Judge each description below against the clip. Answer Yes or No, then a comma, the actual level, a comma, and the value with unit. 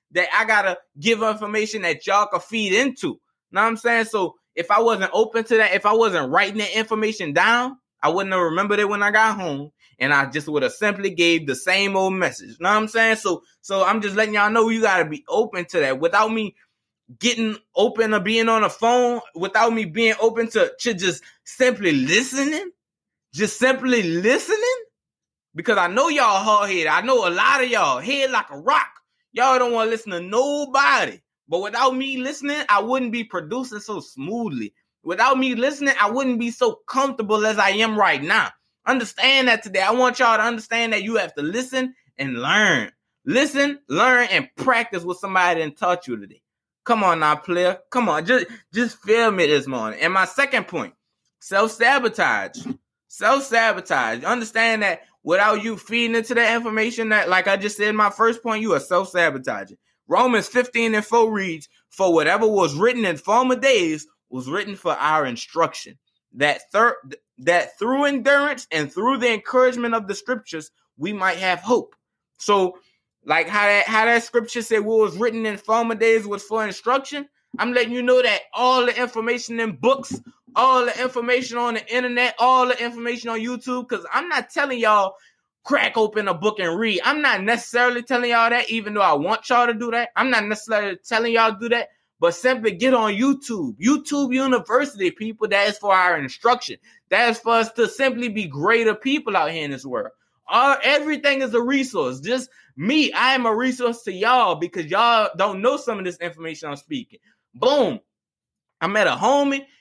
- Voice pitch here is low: No, high, 225 Hz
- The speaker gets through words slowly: No, average, 190 wpm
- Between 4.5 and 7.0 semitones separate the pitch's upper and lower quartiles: No, average, 3.7 semitones